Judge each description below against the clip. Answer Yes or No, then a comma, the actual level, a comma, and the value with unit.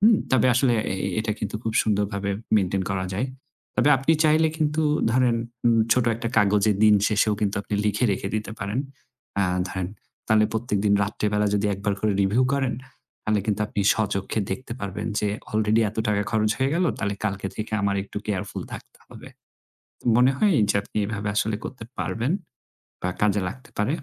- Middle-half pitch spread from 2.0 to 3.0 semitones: Yes, average, 2.7 semitones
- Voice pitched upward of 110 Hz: No, low, 105 Hz